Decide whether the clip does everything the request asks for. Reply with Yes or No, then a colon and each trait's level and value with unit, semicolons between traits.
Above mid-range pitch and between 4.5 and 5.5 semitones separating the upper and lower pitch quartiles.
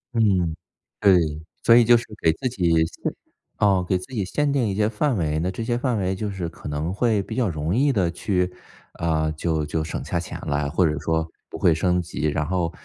No: very low, 90 Hz; average, 5.0 semitones